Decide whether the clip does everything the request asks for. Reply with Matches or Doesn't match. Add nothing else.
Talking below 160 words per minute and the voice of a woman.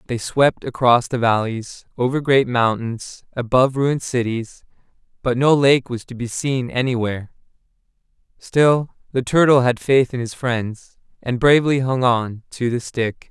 Doesn't match